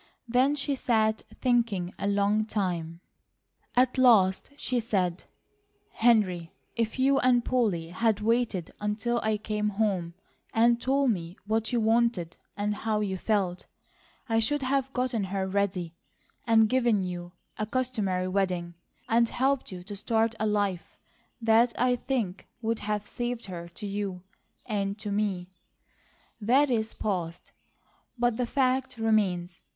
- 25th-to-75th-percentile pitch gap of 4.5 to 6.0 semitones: No, average, 3.9 semitones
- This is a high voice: Yes, high, 215 Hz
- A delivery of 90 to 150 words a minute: Yes, average, 140 wpm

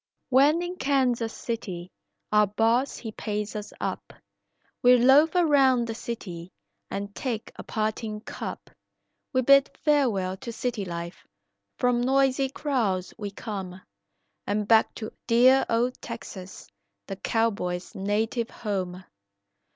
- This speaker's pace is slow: Yes, slow, 125 wpm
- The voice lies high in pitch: Yes, high, 230 Hz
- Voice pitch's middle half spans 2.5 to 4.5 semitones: Yes, average, 4.2 semitones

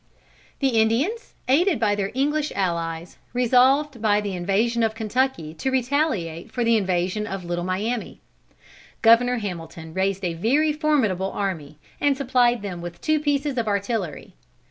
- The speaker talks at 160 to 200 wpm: No, average, 150 wpm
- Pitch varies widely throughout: Yes, wide, 6.1 semitones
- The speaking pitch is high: Yes, high, 220 Hz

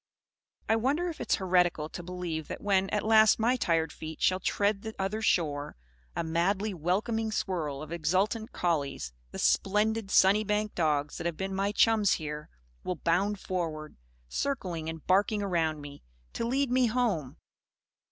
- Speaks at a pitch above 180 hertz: Yes, high, 190 Hz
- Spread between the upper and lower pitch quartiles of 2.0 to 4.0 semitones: No, average, 4.9 semitones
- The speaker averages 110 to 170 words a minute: Yes, average, 160 wpm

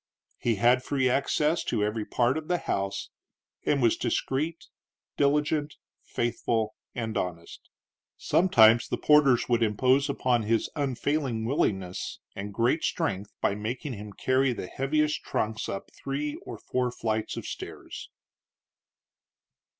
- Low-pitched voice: Yes, low, 125 Hz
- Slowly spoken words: Yes, slow, 130 wpm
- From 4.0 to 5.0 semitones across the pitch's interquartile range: Yes, average, 4.5 semitones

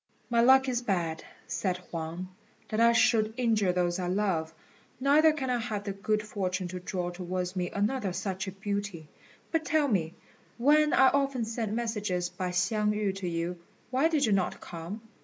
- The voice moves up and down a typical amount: Yes, average, 4.6 semitones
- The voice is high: Yes, high, 200 Hz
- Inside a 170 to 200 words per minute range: Yes, average, 180 wpm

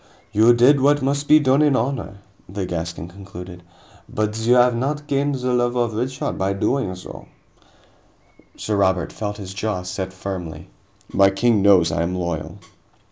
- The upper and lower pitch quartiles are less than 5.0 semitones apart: No, wide, 5.4 semitones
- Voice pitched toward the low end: Yes, low, 105 Hz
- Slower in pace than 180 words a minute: Yes, average, 165 wpm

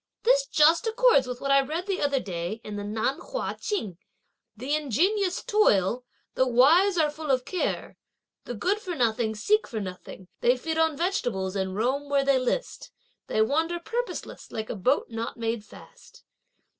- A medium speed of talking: Yes, average, 175 wpm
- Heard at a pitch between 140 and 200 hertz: No, very high, 275 Hz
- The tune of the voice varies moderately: No, wide, 7.7 semitones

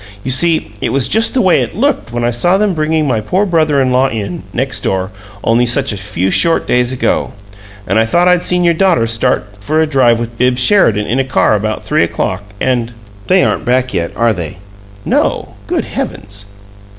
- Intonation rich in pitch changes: Yes, wide, 6.5 semitones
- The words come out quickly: Yes, fast, 210 wpm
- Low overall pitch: Yes, low, 125 Hz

